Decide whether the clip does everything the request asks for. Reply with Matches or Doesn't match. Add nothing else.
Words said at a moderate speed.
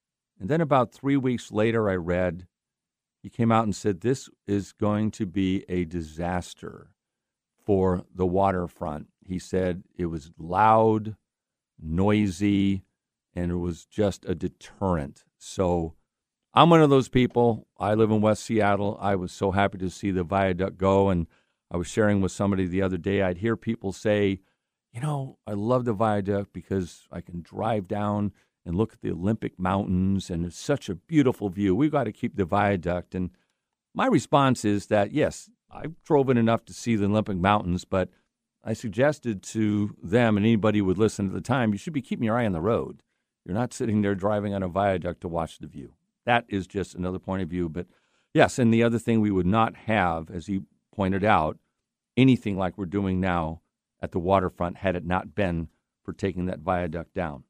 Matches